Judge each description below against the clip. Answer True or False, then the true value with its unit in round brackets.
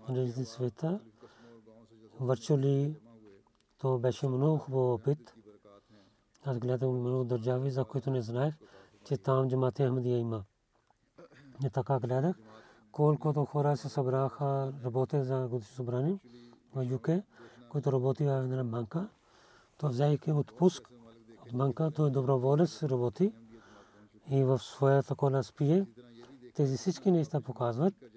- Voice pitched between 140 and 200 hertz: False (130 Hz)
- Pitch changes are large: False (3.0 semitones)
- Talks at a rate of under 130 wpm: True (120 wpm)